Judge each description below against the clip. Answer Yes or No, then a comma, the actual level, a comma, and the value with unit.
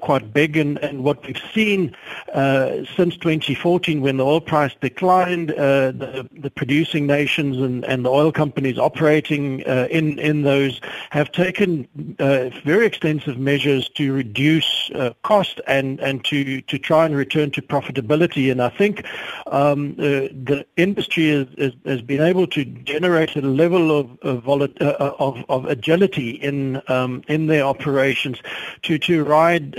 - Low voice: No, medium, 145 Hz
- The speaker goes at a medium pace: Yes, average, 160 wpm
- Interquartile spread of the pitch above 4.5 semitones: No, average, 2.8 semitones